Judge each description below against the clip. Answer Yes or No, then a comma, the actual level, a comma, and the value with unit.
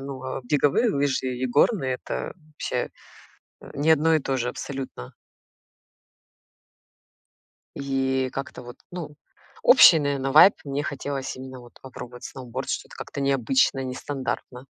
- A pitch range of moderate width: No, narrow, 1.8 semitones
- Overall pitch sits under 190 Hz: Yes, low, 135 Hz